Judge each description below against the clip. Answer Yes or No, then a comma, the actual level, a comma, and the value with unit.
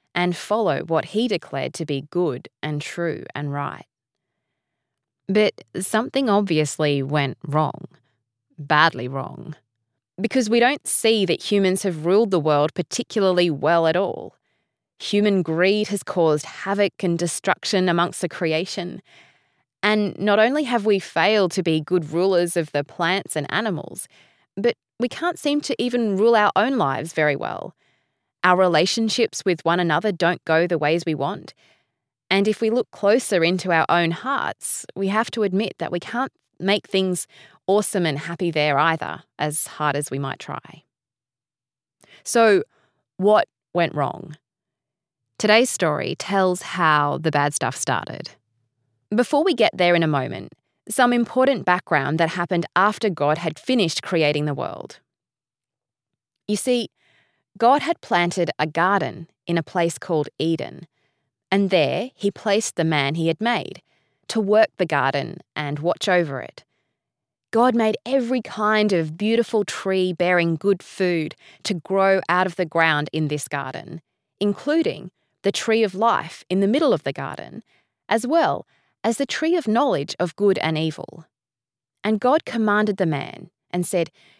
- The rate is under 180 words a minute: Yes, average, 155 wpm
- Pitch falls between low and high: Yes, medium, 175 Hz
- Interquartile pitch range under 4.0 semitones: No, wide, 5.5 semitones